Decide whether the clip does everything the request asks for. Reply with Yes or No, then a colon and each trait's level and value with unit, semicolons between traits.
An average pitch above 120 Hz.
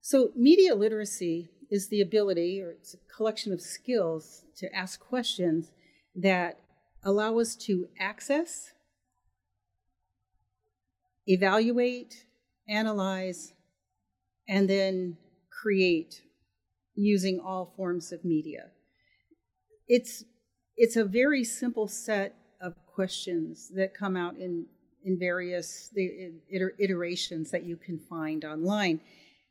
Yes: high, 190 Hz